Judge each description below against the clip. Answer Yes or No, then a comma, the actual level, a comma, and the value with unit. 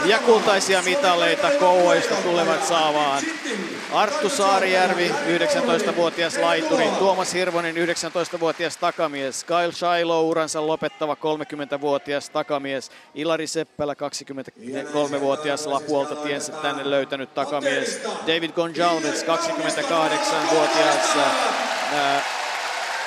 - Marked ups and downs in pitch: No, average, 3.3 semitones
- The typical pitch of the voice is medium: Yes, medium, 160 Hz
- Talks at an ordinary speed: No, slow, 80 wpm